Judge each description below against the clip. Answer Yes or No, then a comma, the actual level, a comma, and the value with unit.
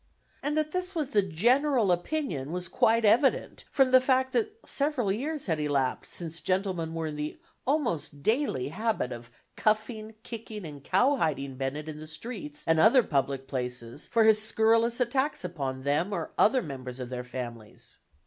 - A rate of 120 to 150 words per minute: No, average, 170 wpm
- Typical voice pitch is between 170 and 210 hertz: Yes, high, 190 Hz